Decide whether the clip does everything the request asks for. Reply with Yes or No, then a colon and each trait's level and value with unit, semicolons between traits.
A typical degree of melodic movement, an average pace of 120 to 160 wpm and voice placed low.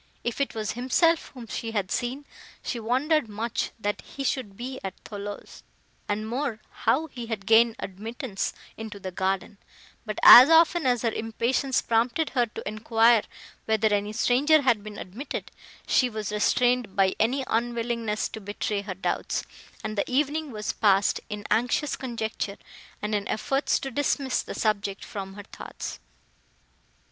No: average, 3.6 semitones; average, 155 wpm; high, 225 Hz